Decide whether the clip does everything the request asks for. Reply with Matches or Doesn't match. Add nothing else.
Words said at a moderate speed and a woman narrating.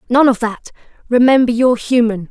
Matches